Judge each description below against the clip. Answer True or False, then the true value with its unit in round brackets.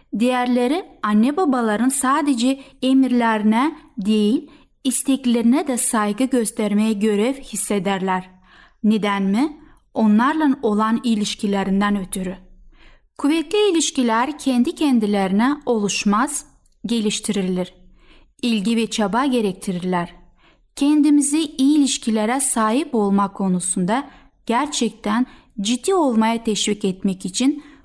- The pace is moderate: False (85 wpm)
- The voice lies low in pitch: False (230 Hz)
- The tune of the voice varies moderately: True (4.4 semitones)